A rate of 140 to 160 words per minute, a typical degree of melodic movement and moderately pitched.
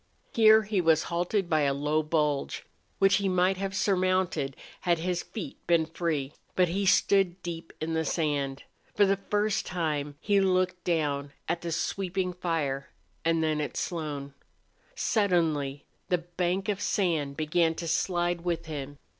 Yes: average, 155 wpm; average, 3.3 semitones; medium, 170 Hz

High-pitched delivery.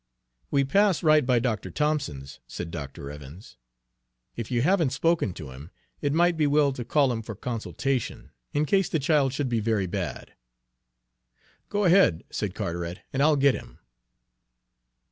No: low, 135 Hz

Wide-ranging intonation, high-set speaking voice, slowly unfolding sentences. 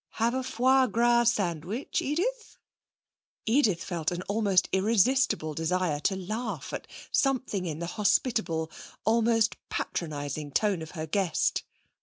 Yes: wide, 5.9 semitones; high, 200 Hz; slow, 125 wpm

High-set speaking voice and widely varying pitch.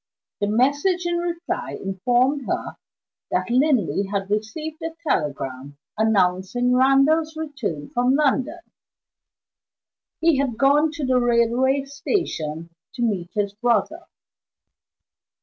Yes: very high, 250 Hz; wide, 6.3 semitones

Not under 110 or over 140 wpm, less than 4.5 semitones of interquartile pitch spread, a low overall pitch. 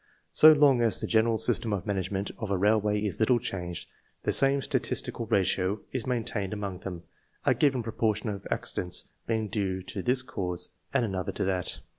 No: average, 180 wpm; average, 3.5 semitones; low, 105 Hz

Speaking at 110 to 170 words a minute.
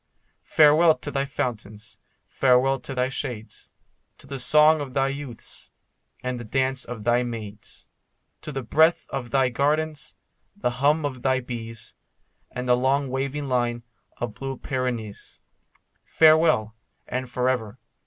Yes: average, 145 wpm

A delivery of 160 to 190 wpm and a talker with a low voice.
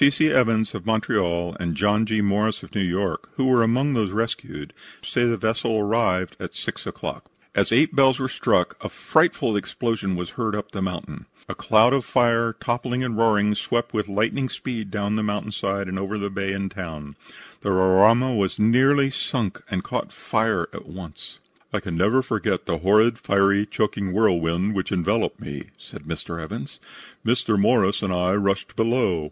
Yes: average, 180 wpm; low, 105 Hz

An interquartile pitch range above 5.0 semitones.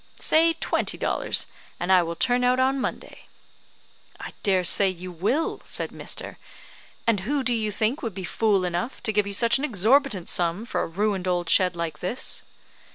Yes: wide, 5.5 semitones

